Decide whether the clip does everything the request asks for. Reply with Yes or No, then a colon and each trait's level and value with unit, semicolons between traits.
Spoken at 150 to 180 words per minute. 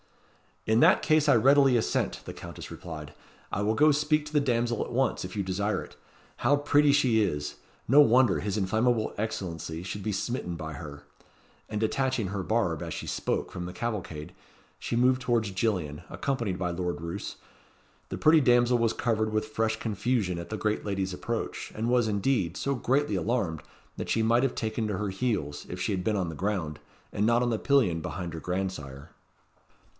No: average, 190 wpm